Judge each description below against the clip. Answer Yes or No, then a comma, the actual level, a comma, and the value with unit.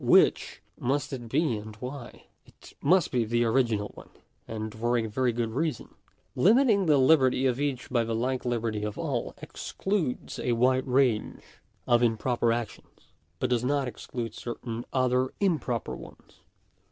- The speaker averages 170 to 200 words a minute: No, average, 155 wpm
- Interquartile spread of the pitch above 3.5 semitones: No, narrow, 2.6 semitones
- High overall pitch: No, low, 125 Hz